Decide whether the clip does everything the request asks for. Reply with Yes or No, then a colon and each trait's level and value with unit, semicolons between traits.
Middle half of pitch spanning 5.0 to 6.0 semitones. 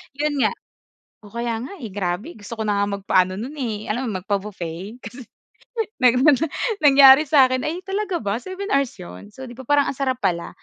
Yes: wide, 5.4 semitones